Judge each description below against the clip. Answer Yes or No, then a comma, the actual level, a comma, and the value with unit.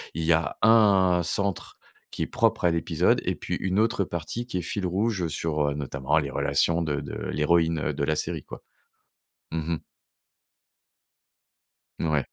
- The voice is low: Yes, very low, 85 Hz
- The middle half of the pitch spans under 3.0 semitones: No, average, 3.4 semitones